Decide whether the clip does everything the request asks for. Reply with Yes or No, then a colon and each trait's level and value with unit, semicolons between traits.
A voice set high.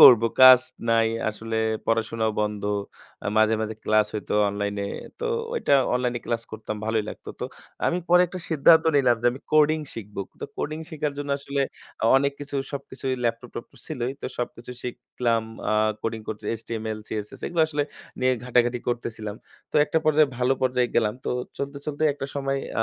No: low, 125 Hz